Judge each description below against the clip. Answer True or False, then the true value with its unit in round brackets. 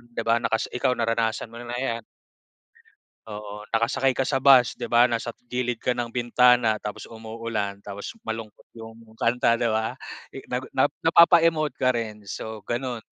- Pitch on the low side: True (115 Hz)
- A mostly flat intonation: True (1.9 semitones)